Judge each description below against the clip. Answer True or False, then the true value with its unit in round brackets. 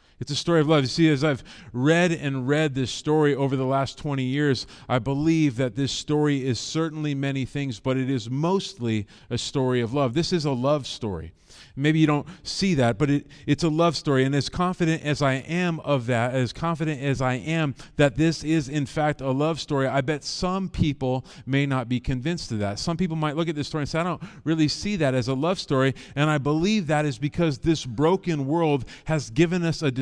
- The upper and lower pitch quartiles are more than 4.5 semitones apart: False (3.3 semitones)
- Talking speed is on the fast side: True (230 wpm)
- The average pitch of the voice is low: False (145 Hz)